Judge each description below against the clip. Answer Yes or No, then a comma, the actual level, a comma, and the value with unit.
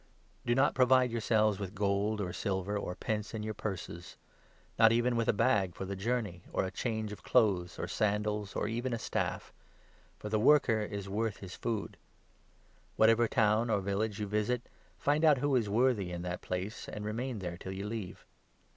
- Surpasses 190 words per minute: Yes, average, 200 wpm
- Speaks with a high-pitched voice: No, low, 105 Hz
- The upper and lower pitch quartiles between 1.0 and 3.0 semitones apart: Yes, average, 2.7 semitones